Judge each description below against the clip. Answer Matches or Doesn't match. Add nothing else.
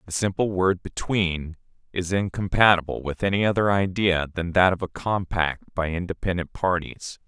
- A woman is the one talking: Doesn't match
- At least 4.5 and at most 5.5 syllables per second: Matches